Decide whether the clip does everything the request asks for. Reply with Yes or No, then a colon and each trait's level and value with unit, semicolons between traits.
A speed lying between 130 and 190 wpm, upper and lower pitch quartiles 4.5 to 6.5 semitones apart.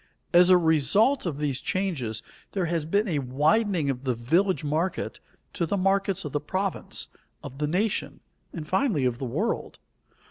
Yes: average, 170 wpm; average, 5.3 semitones